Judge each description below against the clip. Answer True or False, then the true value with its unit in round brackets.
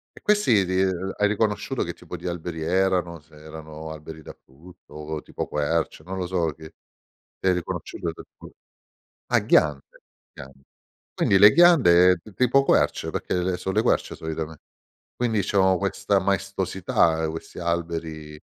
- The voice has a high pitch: False (90 Hz)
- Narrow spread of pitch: False (3.3 semitones)